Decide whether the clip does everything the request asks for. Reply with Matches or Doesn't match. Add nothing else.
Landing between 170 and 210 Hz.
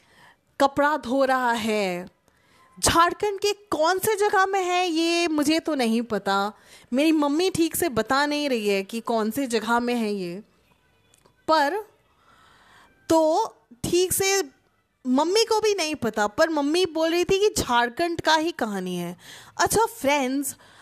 Doesn't match